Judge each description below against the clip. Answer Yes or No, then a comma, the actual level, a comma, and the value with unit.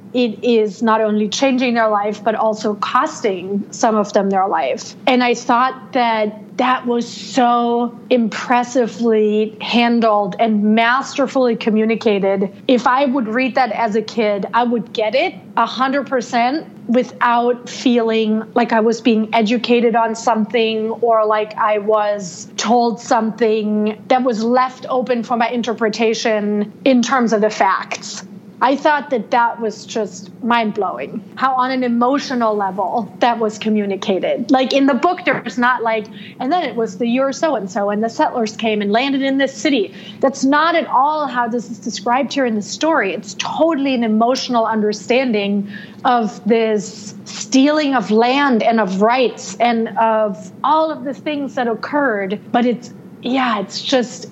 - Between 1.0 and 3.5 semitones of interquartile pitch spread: Yes, average, 2.9 semitones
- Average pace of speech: Yes, average, 160 wpm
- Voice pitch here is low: No, high, 230 Hz